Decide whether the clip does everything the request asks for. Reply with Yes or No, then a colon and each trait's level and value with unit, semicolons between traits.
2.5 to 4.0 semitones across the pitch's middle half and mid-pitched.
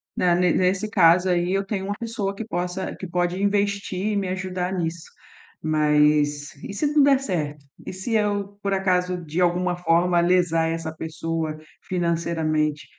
Yes: average, 3.1 semitones; medium, 180 Hz